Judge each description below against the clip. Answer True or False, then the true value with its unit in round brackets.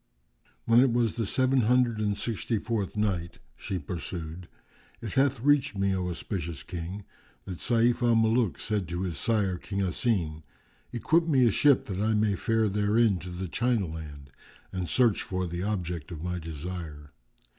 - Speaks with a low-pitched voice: True (100 Hz)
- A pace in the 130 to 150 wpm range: False (170 wpm)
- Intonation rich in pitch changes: False (4.8 semitones)